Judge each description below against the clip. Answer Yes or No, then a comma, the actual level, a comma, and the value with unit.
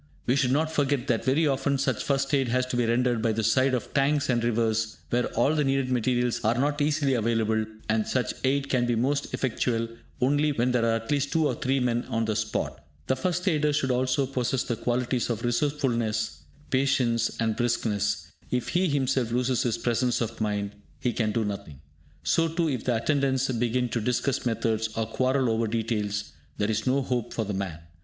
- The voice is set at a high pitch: No, low, 125 Hz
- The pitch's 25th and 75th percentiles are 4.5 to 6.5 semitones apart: No, average, 3.2 semitones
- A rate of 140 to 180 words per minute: No, fast, 205 wpm